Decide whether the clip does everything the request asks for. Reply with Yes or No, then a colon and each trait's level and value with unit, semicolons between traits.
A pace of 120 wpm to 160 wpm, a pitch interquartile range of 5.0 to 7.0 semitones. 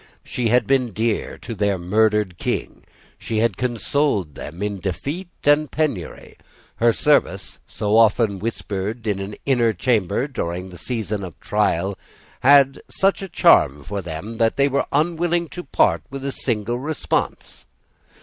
Yes: average, 150 wpm; wide, 5.5 semitones